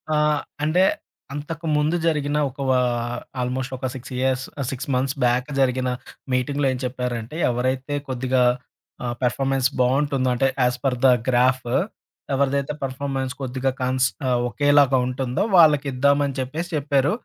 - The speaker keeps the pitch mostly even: Yes, narrow, 1.9 semitones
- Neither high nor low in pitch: No, low, 130 Hz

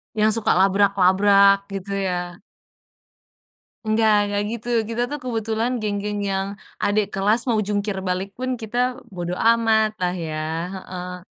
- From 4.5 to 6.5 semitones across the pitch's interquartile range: No, narrow, 2.4 semitones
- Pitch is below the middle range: No, high, 205 Hz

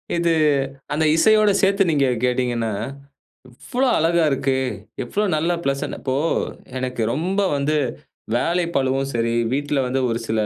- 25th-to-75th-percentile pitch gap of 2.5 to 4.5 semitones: No, average, 5.0 semitones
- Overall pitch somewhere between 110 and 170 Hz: Yes, medium, 140 Hz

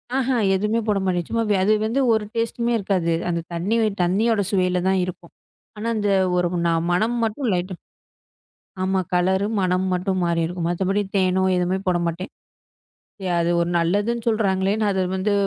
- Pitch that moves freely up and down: No, average, 3.2 semitones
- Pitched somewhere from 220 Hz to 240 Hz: No, high, 190 Hz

